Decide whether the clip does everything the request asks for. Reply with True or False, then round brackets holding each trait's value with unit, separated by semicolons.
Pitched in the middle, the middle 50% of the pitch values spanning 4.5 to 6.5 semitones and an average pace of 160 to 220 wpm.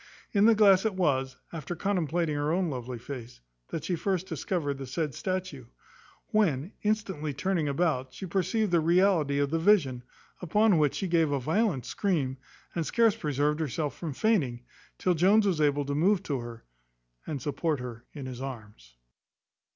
True (155 Hz; 5.4 semitones; 170 wpm)